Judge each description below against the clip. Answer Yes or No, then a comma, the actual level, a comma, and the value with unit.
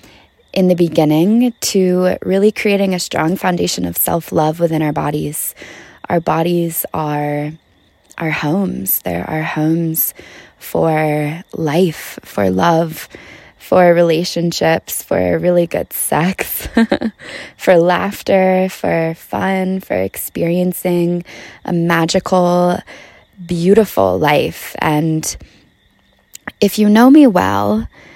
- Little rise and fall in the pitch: No, average, 3.2 semitones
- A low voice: No, medium, 170 Hz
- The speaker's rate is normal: No, slow, 105 wpm